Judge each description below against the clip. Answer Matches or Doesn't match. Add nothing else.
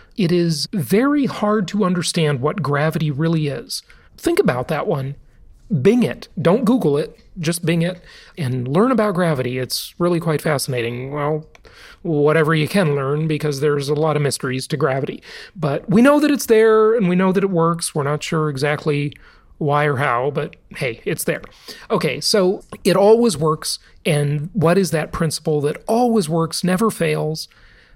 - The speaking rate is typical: Matches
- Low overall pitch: Doesn't match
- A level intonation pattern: Doesn't match